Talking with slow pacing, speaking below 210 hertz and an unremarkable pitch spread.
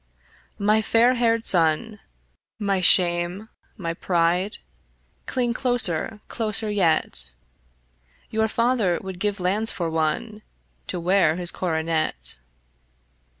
Yes: slow, 105 wpm; high, 190 Hz; average, 4.6 semitones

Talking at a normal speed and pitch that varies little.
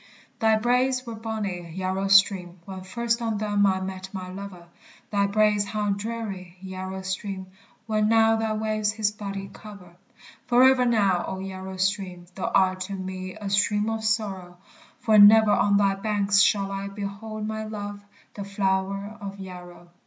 Yes: average, 160 wpm; narrow, 2.3 semitones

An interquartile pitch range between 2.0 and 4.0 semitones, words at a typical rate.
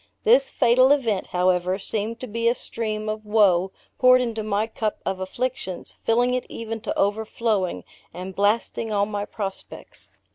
Yes: average, 2.7 semitones; average, 155 wpm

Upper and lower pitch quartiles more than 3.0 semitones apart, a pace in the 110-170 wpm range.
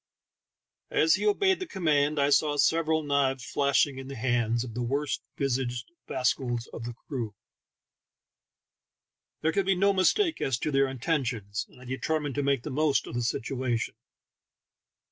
Yes: average, 4.1 semitones; average, 160 wpm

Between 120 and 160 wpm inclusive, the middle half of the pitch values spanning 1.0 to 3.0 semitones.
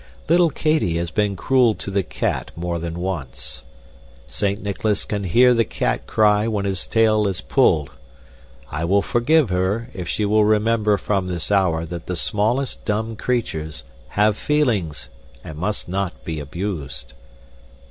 No: average, 155 wpm; average, 4.3 semitones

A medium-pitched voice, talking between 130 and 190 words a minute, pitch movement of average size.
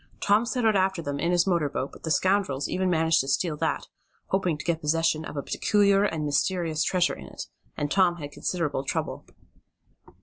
No: medium, 170 Hz; average, 200 wpm; average, 4.1 semitones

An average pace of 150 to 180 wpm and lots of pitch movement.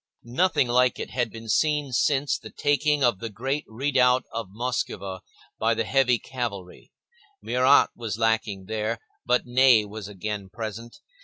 No: average, 155 wpm; average, 3.2 semitones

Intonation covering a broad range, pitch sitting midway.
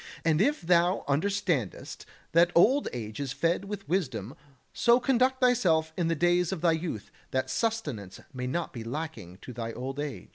Yes: wide, 6.8 semitones; medium, 165 Hz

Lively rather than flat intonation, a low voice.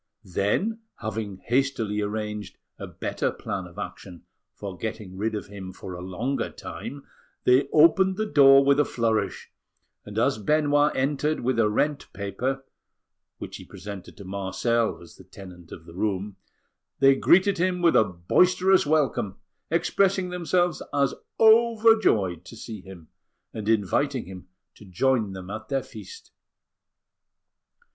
Yes: wide, 7.1 semitones; low, 115 Hz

